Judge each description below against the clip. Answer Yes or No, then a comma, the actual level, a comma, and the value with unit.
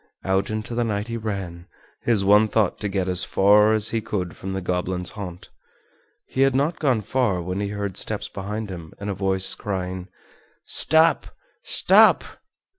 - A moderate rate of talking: Yes, average, 175 wpm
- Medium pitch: No, low, 100 Hz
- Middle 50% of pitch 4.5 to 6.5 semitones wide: No, average, 2.8 semitones